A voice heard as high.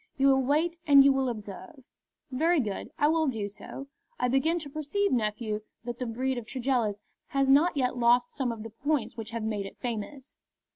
Yes: very high, 255 Hz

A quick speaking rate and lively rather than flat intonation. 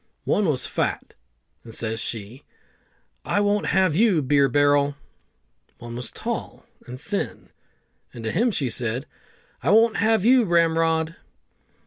No: slow, 135 wpm; wide, 8.3 semitones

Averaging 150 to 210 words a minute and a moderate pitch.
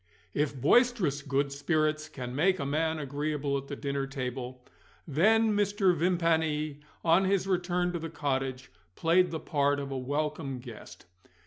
Yes: average, 155 wpm; medium, 150 Hz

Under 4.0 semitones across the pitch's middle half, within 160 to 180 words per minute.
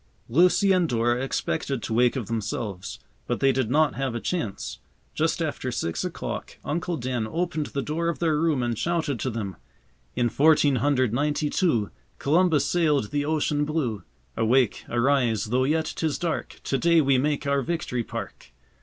No: average, 4.8 semitones; average, 170 wpm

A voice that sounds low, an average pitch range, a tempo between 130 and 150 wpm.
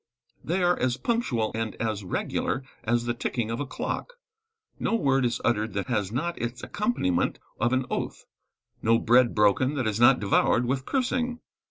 No: low, 120 Hz; average, 3.7 semitones; average, 175 wpm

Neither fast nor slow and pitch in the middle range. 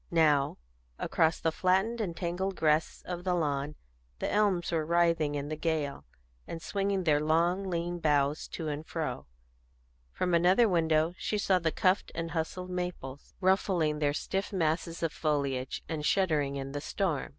Yes: average, 160 wpm; medium, 165 Hz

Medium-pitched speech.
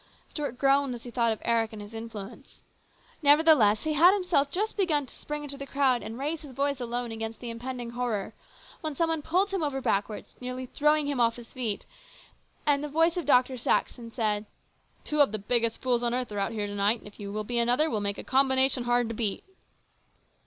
No: very high, 250 Hz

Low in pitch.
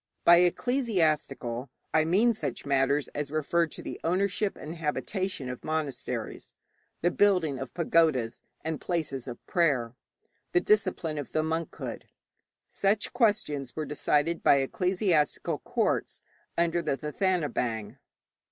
No: medium, 160 Hz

